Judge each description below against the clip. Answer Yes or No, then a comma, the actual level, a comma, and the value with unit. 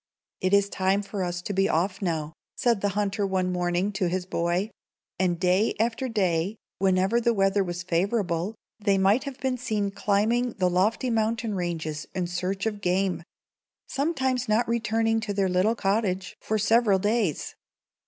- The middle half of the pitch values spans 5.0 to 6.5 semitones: No, average, 3.4 semitones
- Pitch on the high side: Yes, high, 195 Hz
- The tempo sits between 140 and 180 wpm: Yes, average, 170 wpm